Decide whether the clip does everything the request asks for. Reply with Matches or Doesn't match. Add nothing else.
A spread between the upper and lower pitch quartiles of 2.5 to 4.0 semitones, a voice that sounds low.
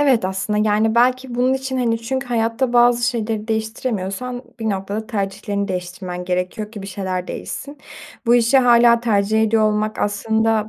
Doesn't match